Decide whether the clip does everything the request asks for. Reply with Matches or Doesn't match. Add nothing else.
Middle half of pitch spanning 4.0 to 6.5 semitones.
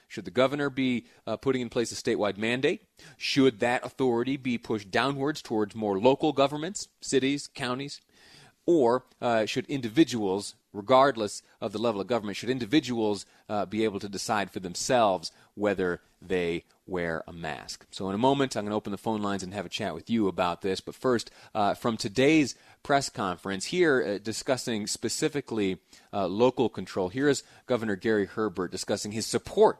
Matches